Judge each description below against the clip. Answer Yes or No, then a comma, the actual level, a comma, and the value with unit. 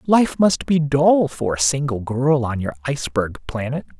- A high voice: No, low, 135 Hz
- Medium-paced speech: Yes, average, 180 wpm